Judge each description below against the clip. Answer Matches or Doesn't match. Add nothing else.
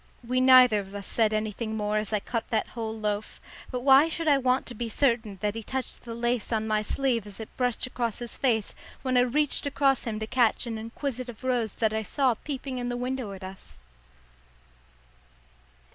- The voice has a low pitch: Doesn't match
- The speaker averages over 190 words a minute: Matches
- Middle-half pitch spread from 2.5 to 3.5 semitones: Matches